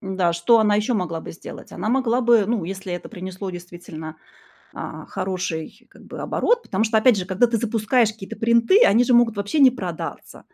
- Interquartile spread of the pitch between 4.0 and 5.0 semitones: Yes, average, 4.3 semitones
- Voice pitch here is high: Yes, high, 210 Hz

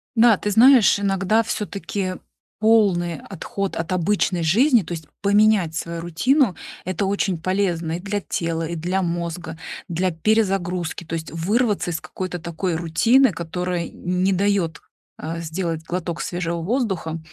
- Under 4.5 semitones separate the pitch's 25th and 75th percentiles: Yes, average, 3.4 semitones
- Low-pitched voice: No, medium, 180 Hz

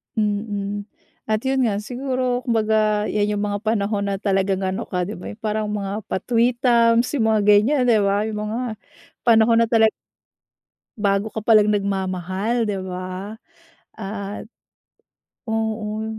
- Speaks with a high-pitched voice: Yes, high, 210 Hz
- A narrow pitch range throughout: Yes, narrow, 2.0 semitones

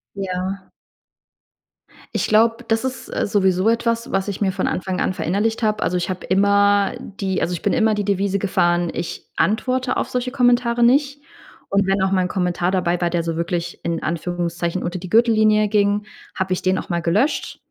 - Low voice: No, high, 195 Hz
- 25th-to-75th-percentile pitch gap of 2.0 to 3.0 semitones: No, average, 3.5 semitones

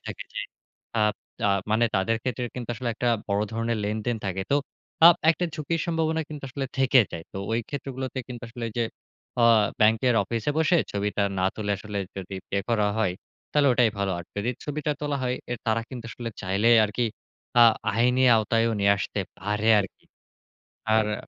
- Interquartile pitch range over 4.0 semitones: No, average, 3.7 semitones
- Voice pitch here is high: No, low, 115 Hz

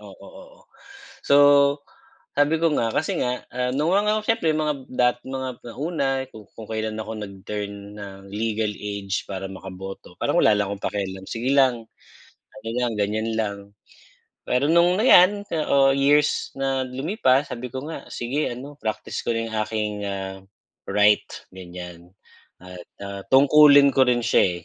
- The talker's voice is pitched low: Yes, low, 120 Hz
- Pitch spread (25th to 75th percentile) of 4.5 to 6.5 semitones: Yes, wide, 5.6 semitones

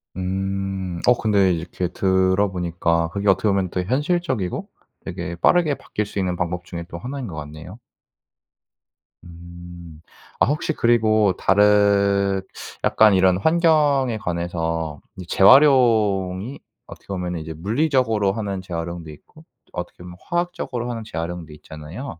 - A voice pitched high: No, very low, 95 Hz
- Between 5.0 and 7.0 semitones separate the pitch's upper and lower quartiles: No, average, 4.4 semitones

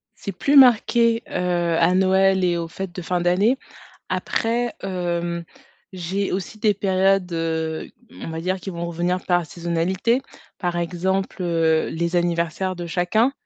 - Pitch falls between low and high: Yes, medium, 180 Hz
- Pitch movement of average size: No, narrow, 2.2 semitones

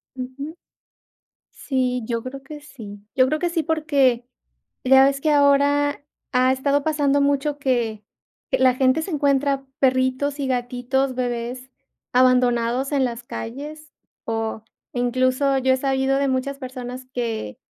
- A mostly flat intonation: Yes, narrow, 2.1 semitones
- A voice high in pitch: Yes, very high, 260 Hz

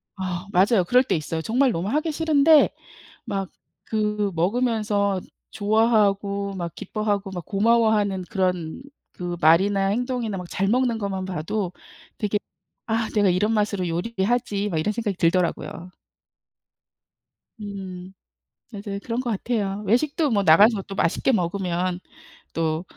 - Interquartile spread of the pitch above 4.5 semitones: No, average, 3.4 semitones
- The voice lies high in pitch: Yes, high, 200 Hz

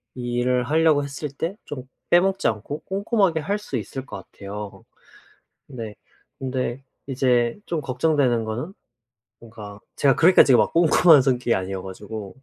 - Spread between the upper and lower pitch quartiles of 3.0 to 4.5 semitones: No, wide, 5.6 semitones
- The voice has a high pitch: No, low, 130 Hz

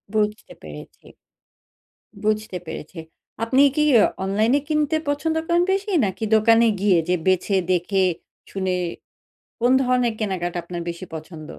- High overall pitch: Yes, high, 210 Hz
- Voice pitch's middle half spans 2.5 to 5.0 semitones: No, wide, 5.5 semitones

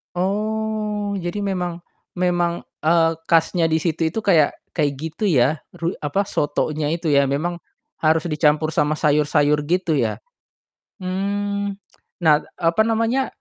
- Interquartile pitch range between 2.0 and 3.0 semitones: No, average, 4.6 semitones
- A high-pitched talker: No, medium, 170 Hz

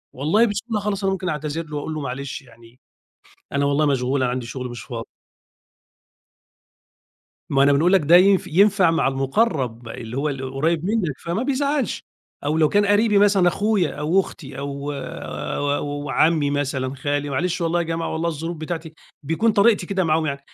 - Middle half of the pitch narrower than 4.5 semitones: No, average, 5.2 semitones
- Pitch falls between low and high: Yes, medium, 155 Hz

